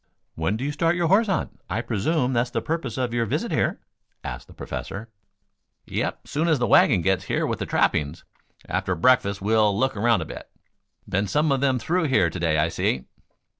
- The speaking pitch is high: No, low, 120 Hz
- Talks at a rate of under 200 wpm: No, fast, 205 wpm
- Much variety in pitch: Yes, wide, 6.9 semitones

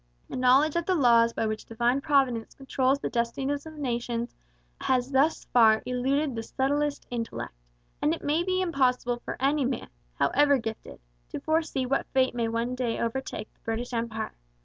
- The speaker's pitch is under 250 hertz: No, very high, 255 Hz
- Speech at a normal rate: Yes, average, 170 wpm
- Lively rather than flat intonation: No, average, 3.3 semitones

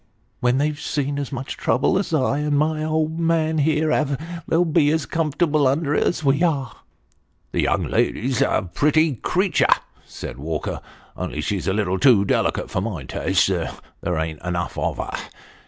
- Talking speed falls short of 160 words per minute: No, average, 185 wpm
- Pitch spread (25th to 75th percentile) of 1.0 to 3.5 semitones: No, average, 4.7 semitones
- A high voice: No, medium, 145 Hz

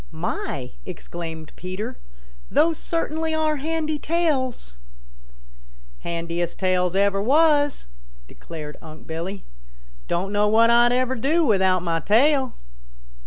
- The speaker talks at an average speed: No, slow, 115 wpm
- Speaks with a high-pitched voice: Yes, high, 220 Hz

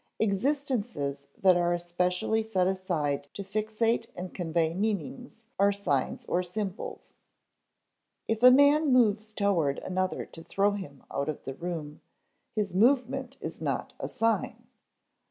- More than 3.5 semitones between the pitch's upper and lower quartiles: Yes, average, 4.4 semitones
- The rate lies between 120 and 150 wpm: Yes, slow, 135 wpm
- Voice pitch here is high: Yes, high, 195 Hz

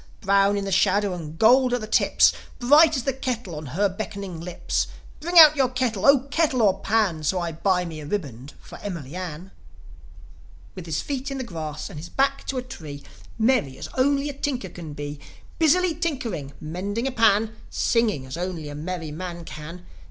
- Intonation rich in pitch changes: Yes, wide, 7.6 semitones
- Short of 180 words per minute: No, average, 195 wpm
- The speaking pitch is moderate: No, high, 195 Hz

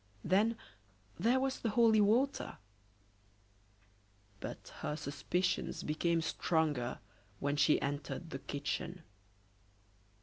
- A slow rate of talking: Yes, slow, 95 wpm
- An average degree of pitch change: No, wide, 7.1 semitones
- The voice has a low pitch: No, medium, 170 Hz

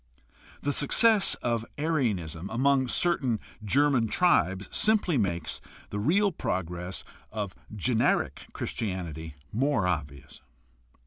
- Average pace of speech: No, slow, 100 wpm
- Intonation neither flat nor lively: No, wide, 8.0 semitones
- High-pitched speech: No, low, 110 Hz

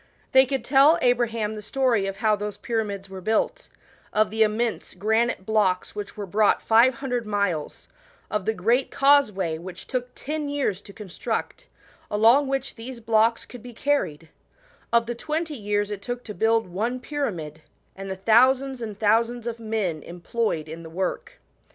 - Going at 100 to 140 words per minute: No, average, 175 wpm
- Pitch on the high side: Yes, high, 220 Hz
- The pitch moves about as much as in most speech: Yes, average, 3.7 semitones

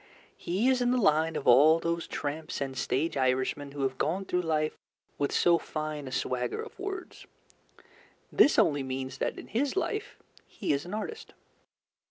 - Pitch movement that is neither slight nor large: No, wide, 6.1 semitones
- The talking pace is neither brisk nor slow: Yes, average, 175 wpm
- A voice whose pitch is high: No, medium, 155 Hz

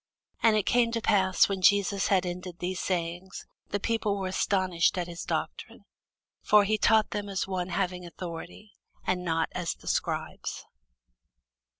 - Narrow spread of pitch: Yes, narrow, 2.2 semitones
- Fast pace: No, average, 160 wpm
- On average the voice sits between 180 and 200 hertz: Yes, medium, 185 Hz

